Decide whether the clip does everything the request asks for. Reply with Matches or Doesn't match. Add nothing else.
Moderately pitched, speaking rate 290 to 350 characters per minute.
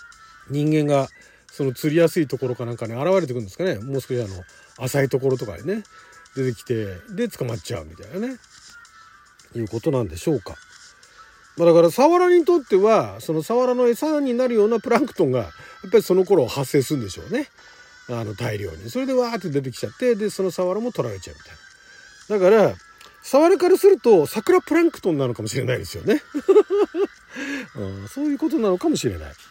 Doesn't match